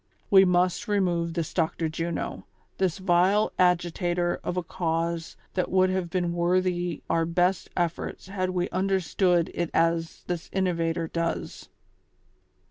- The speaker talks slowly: Yes, slow, 130 wpm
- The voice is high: No, medium, 175 Hz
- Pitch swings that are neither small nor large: No, narrow, 1.7 semitones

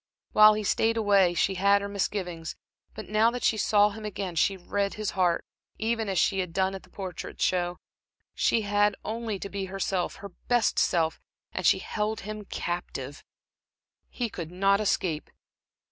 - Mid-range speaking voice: No, high, 200 Hz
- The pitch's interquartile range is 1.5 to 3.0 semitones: Yes, average, 2.7 semitones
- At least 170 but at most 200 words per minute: Yes, average, 175 wpm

